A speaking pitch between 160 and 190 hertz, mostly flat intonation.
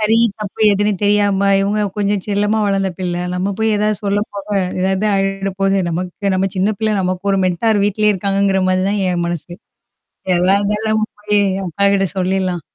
No: high, 200 Hz; narrow, 1.7 semitones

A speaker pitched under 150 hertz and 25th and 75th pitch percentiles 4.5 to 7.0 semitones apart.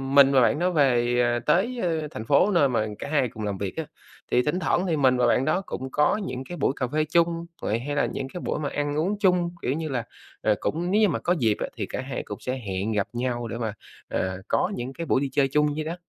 Yes: medium, 140 Hz; wide, 5.4 semitones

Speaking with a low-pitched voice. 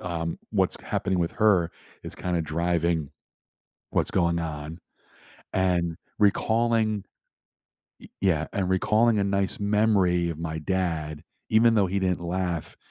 Yes: very low, 90 Hz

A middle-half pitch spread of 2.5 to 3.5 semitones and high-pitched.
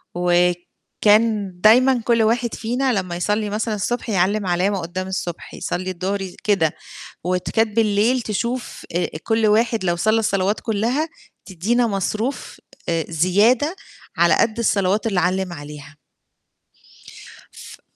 No: average, 3.9 semitones; high, 205 Hz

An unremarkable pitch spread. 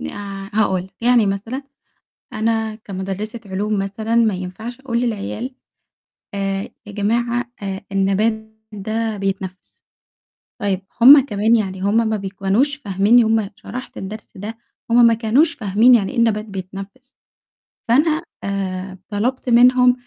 Yes: average, 3.2 semitones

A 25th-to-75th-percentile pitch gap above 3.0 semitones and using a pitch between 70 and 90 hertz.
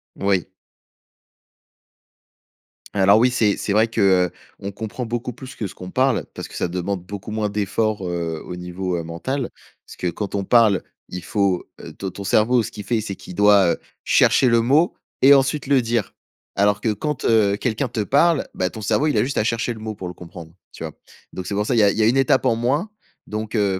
No: average, 4.0 semitones; low, 105 Hz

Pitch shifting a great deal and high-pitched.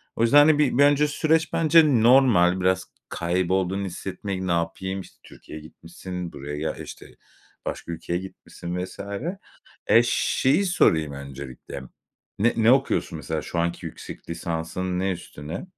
No: wide, 6.5 semitones; very low, 95 Hz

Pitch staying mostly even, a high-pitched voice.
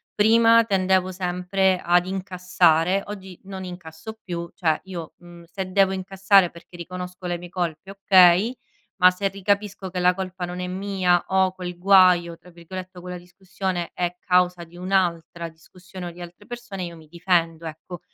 No: narrow, 1.6 semitones; medium, 180 Hz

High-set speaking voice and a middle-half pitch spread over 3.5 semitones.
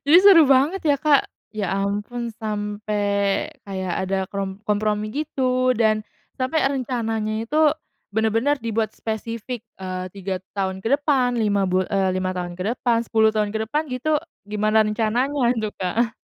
Yes: high, 220 Hz; average, 3.9 semitones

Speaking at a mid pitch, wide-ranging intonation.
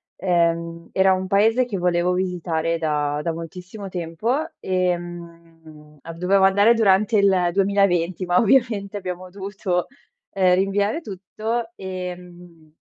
No: medium, 180 Hz; average, 2.8 semitones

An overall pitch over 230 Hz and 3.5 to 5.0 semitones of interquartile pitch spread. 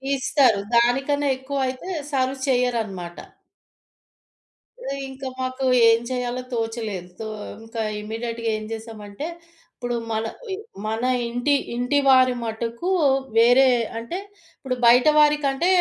No: high, 245 Hz; average, 2.9 semitones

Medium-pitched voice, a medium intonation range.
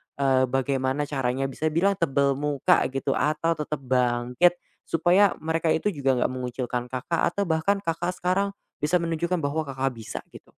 Yes: medium, 145 Hz; average, 4.2 semitones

